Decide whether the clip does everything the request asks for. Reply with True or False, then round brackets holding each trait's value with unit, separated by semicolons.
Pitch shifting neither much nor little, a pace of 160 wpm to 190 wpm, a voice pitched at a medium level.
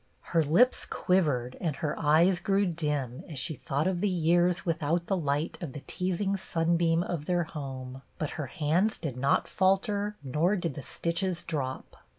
True (3.9 semitones; 170 wpm; 165 Hz)